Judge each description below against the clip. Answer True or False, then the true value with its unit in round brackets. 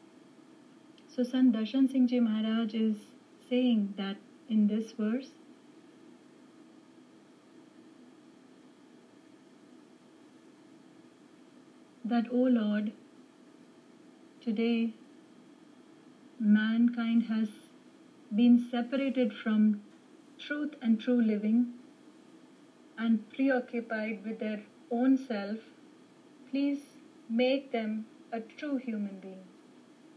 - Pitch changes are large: False (4.7 semitones)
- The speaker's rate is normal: False (80 wpm)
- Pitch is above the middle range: True (280 Hz)